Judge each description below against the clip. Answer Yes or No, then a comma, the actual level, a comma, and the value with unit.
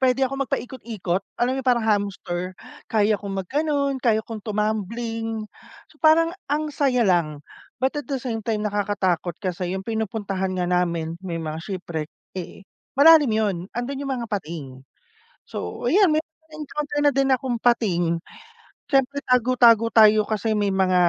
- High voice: Yes, high, 220 Hz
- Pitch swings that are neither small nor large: No, wide, 5.9 semitones